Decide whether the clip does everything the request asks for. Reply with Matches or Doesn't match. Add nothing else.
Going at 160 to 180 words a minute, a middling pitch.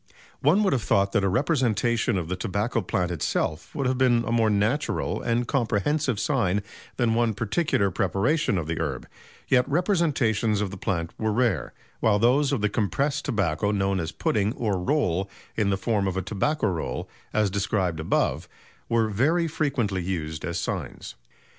Doesn't match